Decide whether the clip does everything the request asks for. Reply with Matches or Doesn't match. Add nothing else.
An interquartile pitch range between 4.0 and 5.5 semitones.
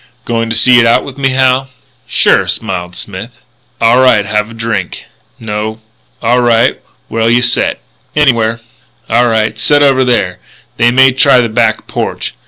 Doesn't match